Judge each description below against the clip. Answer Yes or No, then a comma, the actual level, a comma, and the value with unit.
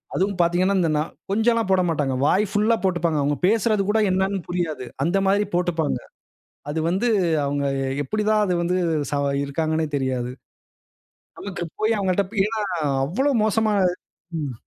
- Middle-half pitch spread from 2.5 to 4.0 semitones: No, average, 4.7 semitones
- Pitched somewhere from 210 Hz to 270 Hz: No, medium, 185 Hz